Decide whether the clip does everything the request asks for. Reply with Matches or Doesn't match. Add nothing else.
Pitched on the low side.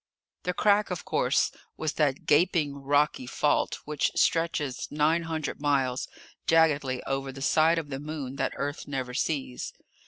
Doesn't match